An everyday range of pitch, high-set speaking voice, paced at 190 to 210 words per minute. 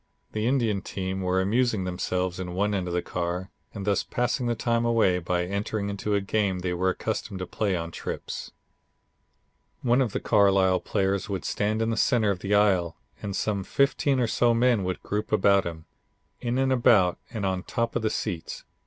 No: average, 3.4 semitones; low, 100 Hz; average, 195 wpm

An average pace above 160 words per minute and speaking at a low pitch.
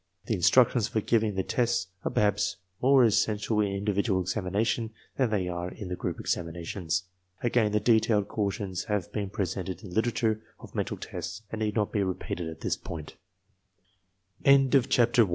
No: average, 150 wpm; low, 105 Hz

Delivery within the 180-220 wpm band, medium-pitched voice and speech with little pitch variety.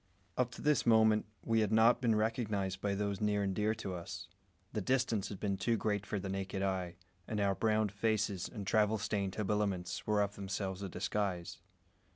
No: average, 195 wpm; low, 105 Hz; narrow, 2.1 semitones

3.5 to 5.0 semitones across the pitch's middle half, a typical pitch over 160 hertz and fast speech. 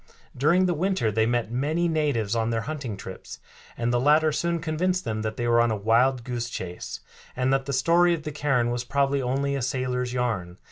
No: average, 4.5 semitones; low, 130 Hz; fast, 215 wpm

